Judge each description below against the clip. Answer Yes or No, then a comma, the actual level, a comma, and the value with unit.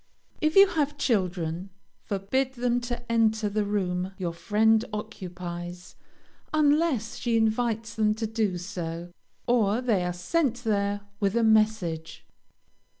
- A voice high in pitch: Yes, high, 215 Hz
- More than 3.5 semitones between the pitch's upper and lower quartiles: Yes, average, 4.5 semitones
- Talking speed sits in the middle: No, slow, 130 wpm